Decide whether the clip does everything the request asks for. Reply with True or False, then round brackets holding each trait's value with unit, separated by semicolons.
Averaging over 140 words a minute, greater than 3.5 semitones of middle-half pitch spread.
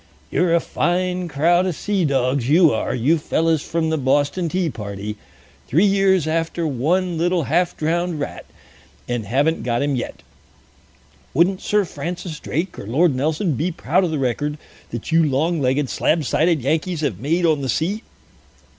True (170 wpm; 4.1 semitones)